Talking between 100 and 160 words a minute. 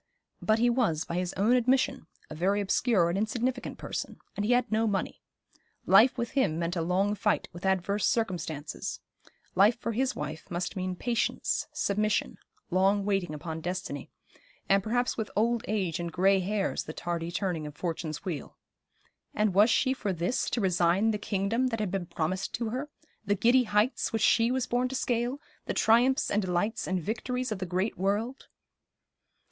No: average, 180 wpm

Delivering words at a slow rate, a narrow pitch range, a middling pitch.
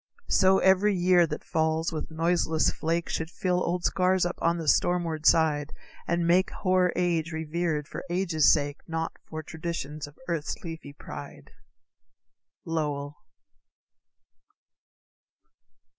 Yes: slow, 125 wpm; narrow, 2.1 semitones; medium, 165 Hz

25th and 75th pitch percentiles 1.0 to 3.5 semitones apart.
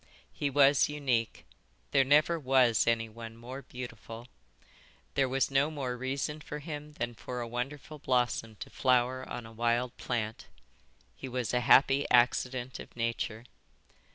Yes: average, 2.7 semitones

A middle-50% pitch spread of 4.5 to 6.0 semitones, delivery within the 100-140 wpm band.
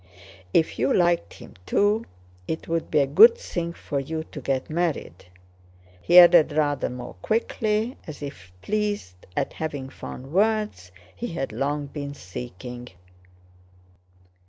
Yes: average, 5.3 semitones; slow, 135 wpm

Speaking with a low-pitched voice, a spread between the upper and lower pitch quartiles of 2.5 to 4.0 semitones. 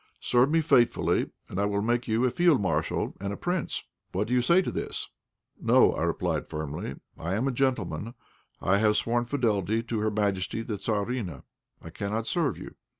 Yes: low, 110 Hz; average, 3.7 semitones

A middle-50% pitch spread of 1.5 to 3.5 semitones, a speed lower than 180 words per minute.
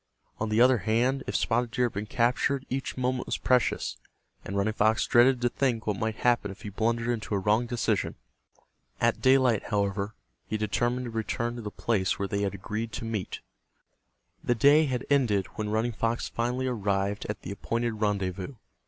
No: average, 2.9 semitones; average, 190 wpm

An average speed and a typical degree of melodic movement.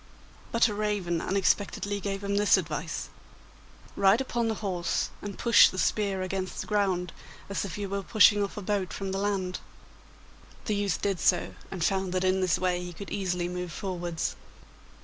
No: average, 180 wpm; narrow, 2.0 semitones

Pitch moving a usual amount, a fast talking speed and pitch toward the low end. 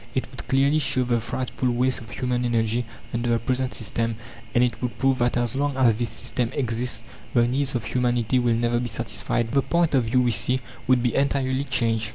No: narrow, 1.9 semitones; fast, 215 wpm; low, 125 Hz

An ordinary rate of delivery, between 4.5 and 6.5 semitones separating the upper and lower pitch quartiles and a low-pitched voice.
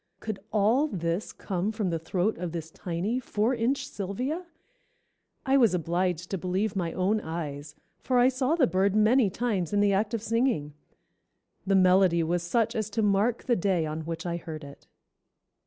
No: average, 180 wpm; average, 4.9 semitones; high, 195 Hz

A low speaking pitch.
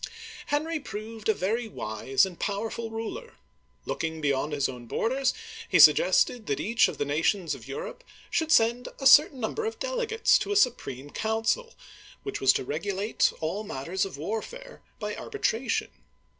No: high, 225 Hz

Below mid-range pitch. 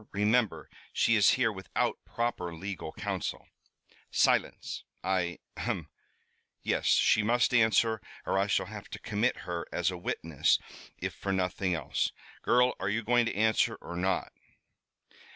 Yes: low, 100 Hz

